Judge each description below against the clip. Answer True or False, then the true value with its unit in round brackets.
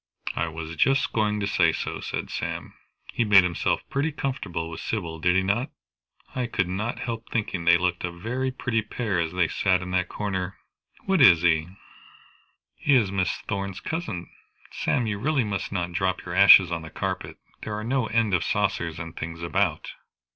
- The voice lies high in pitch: False (95 Hz)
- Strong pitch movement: False (4.7 semitones)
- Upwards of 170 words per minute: True (190 wpm)